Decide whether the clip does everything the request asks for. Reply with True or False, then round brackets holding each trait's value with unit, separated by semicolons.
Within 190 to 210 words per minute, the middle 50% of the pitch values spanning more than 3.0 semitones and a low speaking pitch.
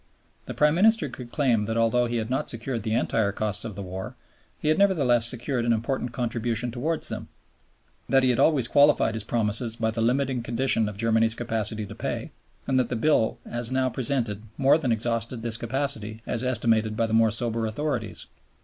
False (195 wpm; 2.6 semitones; 115 Hz)